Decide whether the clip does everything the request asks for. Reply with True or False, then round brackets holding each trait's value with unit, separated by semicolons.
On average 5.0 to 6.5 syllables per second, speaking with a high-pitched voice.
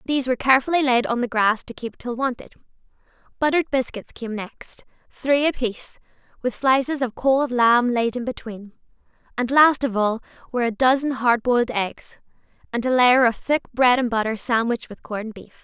True (5.4 syllables/s; 245 Hz)